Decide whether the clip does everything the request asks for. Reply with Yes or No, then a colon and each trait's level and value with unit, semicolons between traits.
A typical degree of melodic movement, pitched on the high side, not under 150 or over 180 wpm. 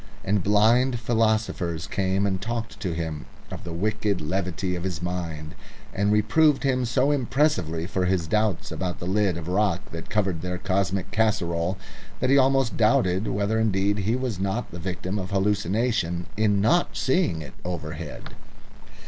No: average, 3.9 semitones; low, 100 Hz; average, 160 wpm